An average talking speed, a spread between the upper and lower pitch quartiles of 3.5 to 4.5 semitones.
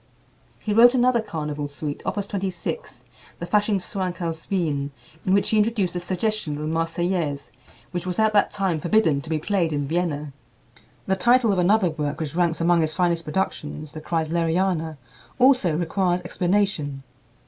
Yes: average, 160 wpm; average, 4.0 semitones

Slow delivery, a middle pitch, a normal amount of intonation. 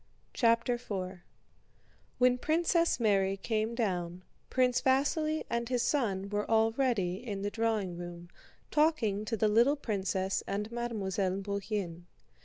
No: slow, 125 wpm; high, 215 Hz; average, 4.2 semitones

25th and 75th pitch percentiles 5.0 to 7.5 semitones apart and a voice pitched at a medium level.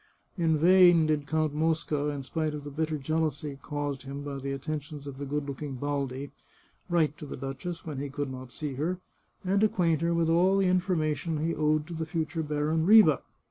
No: narrow, 2.5 semitones; medium, 155 Hz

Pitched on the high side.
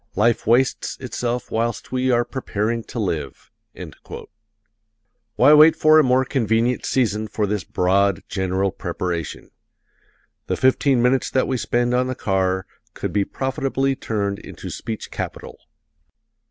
No: low, 120 Hz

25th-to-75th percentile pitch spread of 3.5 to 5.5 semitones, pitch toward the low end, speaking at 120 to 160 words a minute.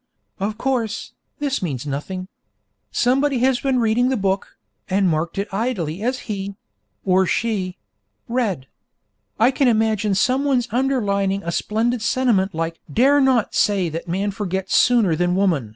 No: average, 4.9 semitones; high, 205 Hz; average, 145 wpm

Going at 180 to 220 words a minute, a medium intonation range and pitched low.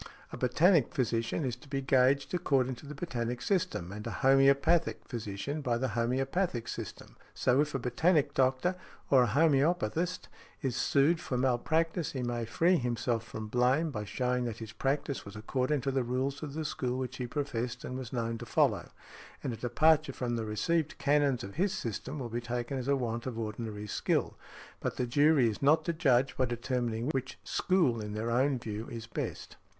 Yes: average, 190 wpm; average, 3.5 semitones; low, 130 Hz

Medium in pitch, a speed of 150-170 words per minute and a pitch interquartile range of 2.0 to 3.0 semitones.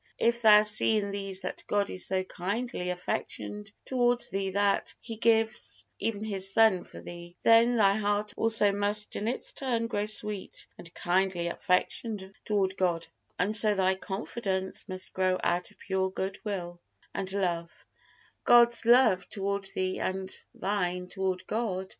No: high, 200 Hz; average, 155 wpm; narrow, 2.4 semitones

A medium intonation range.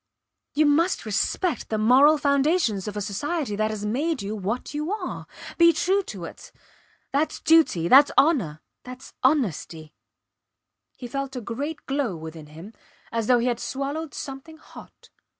No: wide, 6.3 semitones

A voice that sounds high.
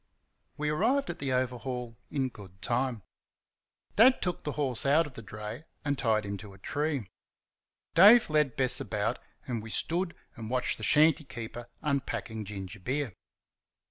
No: low, 130 Hz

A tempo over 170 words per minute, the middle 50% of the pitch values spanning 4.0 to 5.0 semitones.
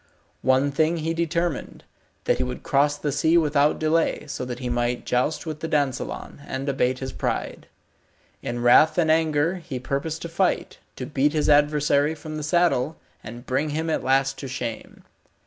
No: average, 180 wpm; average, 3.3 semitones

